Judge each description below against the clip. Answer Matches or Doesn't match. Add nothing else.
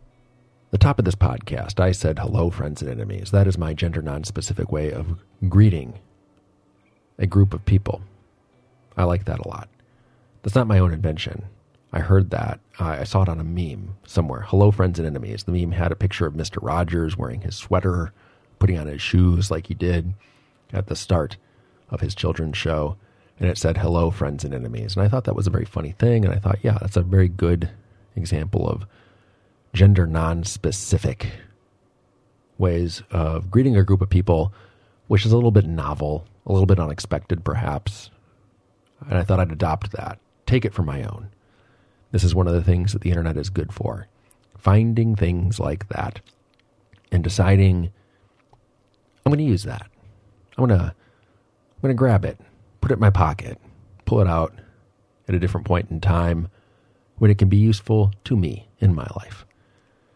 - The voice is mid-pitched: Doesn't match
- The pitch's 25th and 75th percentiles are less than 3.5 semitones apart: Matches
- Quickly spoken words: Doesn't match